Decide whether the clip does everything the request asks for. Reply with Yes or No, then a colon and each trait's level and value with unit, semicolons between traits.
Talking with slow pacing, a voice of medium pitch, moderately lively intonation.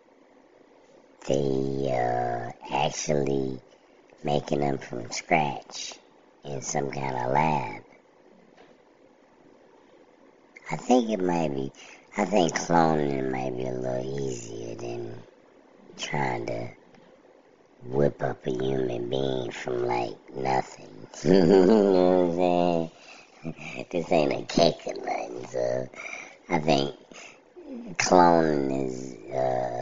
No: slow, 105 wpm; very low, 70 Hz; average, 4.1 semitones